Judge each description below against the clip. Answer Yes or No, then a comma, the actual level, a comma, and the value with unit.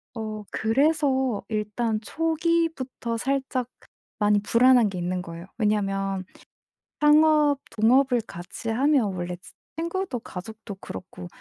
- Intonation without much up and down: No, wide, 5.4 semitones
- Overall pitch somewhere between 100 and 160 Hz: No, high, 230 Hz